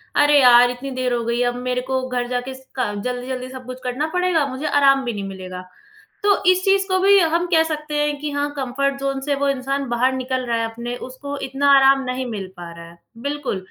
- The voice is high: Yes, very high, 260 Hz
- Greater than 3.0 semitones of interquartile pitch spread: No, average, 2.7 semitones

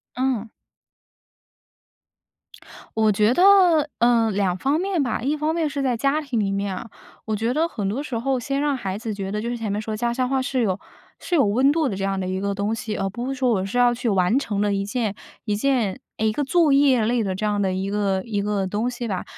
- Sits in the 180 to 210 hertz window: No, high, 225 Hz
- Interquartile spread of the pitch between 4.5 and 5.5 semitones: Yes, average, 4.8 semitones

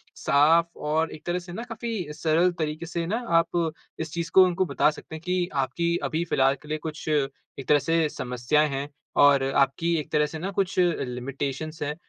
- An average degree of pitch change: Yes, average, 3.0 semitones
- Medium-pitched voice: Yes, medium, 155 Hz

